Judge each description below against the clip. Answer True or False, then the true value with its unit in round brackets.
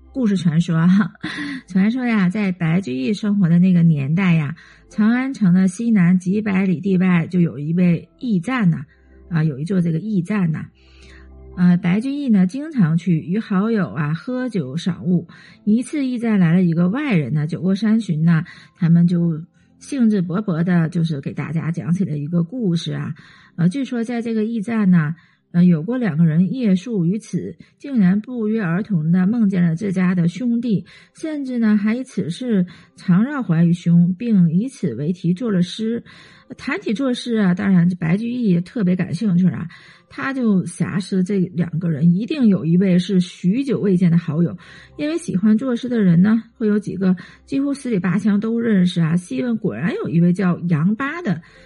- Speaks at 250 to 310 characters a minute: True (265 characters per minute)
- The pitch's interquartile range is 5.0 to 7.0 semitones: False (4.1 semitones)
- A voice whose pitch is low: False (185 Hz)